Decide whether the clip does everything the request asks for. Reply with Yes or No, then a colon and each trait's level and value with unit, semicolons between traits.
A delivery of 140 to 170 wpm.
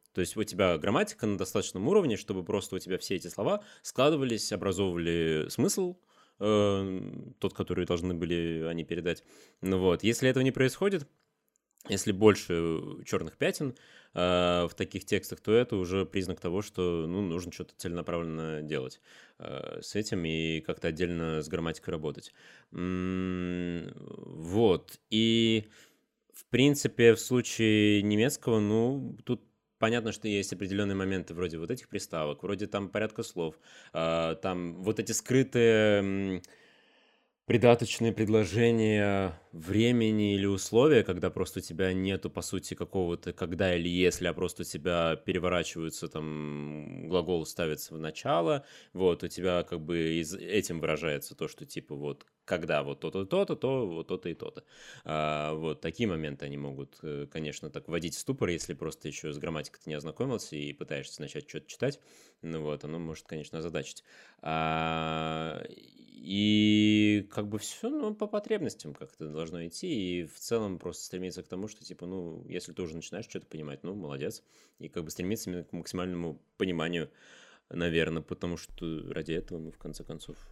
Yes: average, 150 wpm